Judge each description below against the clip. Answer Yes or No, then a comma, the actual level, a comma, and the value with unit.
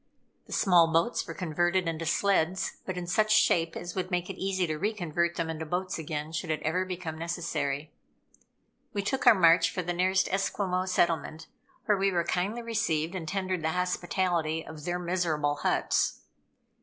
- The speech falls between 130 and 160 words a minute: No, average, 180 wpm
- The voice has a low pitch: No, medium, 175 Hz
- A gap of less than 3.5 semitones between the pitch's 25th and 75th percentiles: Yes, narrow, 2.5 semitones